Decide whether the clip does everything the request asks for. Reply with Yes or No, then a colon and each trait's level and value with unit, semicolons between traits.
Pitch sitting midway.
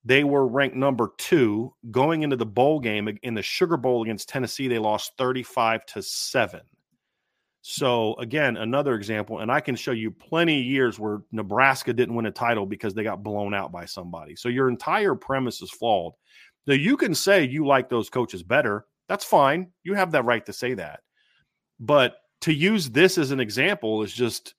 No: low, 125 Hz